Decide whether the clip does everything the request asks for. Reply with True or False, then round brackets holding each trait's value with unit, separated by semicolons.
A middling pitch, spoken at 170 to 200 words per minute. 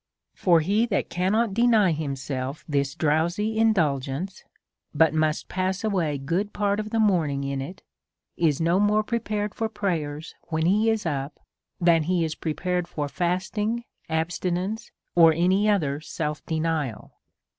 False (175 Hz; 145 wpm)